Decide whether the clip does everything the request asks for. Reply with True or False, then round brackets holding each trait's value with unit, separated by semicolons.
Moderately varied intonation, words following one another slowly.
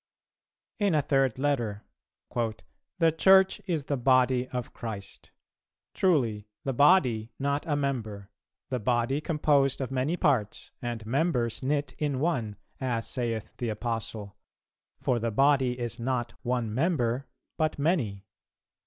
True (3.9 semitones; 130 wpm)